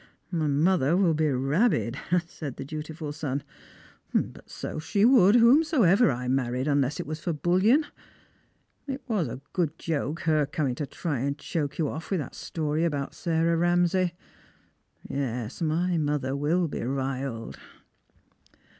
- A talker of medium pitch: Yes, medium, 155 Hz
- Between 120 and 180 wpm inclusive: Yes, average, 155 wpm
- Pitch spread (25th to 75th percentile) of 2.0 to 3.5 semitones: No, average, 4.1 semitones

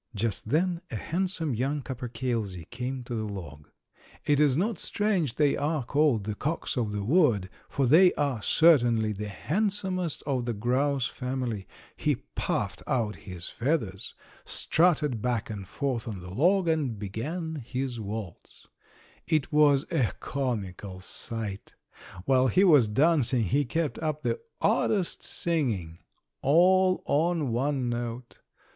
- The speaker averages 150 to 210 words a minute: No, average, 140 wpm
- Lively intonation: Yes, wide, 6.1 semitones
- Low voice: Yes, low, 130 Hz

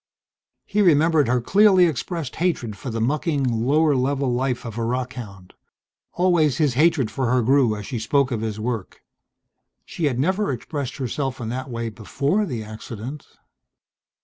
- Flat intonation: No, average, 4.6 semitones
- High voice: No, low, 130 Hz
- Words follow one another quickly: No, average, 160 wpm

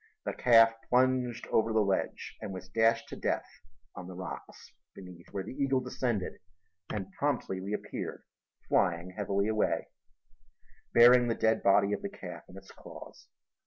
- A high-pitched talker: No, low, 105 Hz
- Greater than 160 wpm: No, average, 155 wpm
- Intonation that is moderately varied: Yes, average, 4.3 semitones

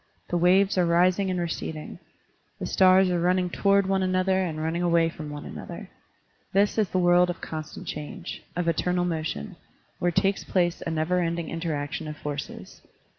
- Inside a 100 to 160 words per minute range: No, average, 175 wpm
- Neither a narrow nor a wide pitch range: No, narrow, 2.3 semitones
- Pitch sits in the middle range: Yes, medium, 175 Hz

